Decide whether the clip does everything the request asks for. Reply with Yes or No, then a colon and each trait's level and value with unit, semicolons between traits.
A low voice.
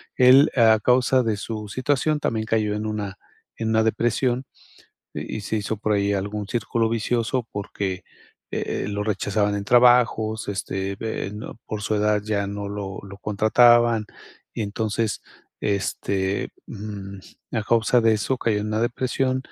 Yes: low, 110 Hz